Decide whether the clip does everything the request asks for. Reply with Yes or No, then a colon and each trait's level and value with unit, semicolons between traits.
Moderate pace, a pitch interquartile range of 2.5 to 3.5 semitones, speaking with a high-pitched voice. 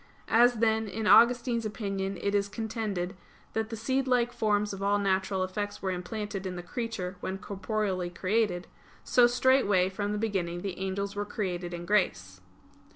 Yes: average, 160 wpm; average, 2.9 semitones; high, 205 Hz